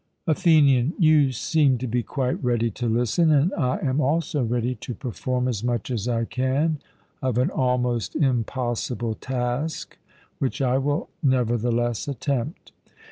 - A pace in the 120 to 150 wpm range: Yes, average, 140 wpm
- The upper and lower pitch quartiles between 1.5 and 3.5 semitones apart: Yes, average, 3.1 semitones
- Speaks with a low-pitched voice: Yes, low, 125 Hz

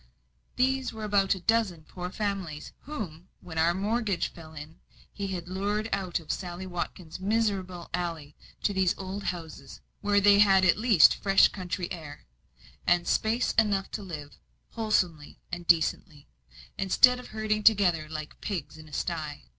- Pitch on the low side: No, medium, 185 Hz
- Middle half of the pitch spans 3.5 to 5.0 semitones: Yes, average, 3.8 semitones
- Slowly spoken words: No, average, 155 wpm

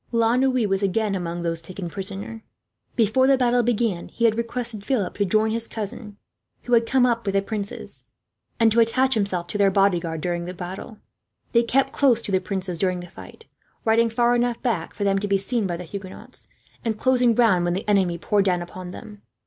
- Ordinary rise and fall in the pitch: Yes, average, 3.9 semitones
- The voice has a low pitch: No, high, 210 Hz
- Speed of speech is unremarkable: No, fast, 210 wpm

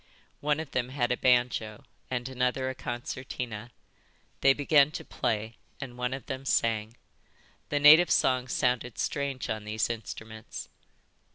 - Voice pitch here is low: Yes, low, 125 Hz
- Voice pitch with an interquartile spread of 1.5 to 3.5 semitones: Yes, average, 2.7 semitones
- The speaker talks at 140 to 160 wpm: Yes, average, 145 wpm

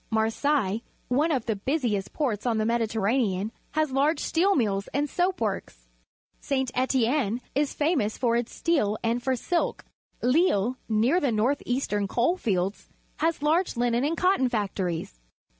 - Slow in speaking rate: No, average, 155 wpm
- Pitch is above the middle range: Yes, high, 245 Hz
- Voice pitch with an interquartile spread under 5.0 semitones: No, wide, 5.4 semitones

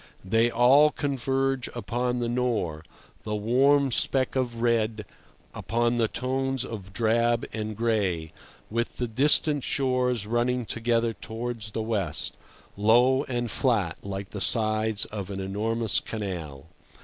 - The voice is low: Yes, low, 115 Hz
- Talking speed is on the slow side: Yes, slow, 130 wpm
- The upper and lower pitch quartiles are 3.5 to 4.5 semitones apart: No, average, 2.7 semitones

